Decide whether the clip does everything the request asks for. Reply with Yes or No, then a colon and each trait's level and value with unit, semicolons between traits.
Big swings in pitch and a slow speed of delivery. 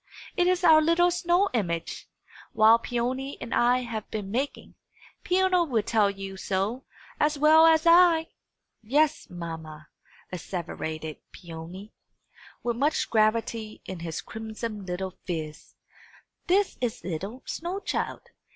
Yes: wide, 8.6 semitones; slow, 125 wpm